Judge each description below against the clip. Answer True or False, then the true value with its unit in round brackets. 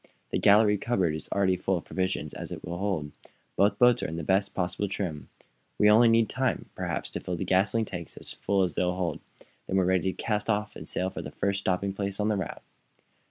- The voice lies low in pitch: True (95 Hz)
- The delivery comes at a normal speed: False (235 wpm)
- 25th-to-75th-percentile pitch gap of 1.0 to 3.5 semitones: True (2.4 semitones)